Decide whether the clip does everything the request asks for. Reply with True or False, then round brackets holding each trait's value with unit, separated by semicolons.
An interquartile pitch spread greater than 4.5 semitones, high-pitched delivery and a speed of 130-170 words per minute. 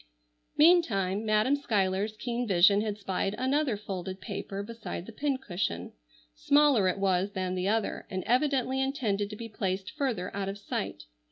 True (4.9 semitones; 210 Hz; 155 wpm)